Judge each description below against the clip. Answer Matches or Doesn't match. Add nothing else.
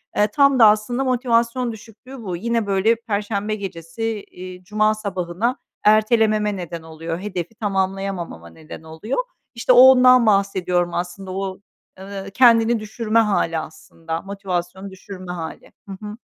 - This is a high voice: Matches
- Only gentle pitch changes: Doesn't match